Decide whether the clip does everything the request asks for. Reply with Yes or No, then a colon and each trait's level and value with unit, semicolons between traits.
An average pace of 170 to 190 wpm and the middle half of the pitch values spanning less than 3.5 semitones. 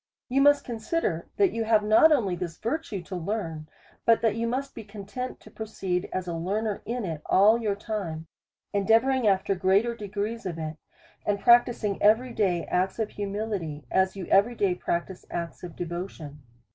No: average, 175 wpm; average, 4.1 semitones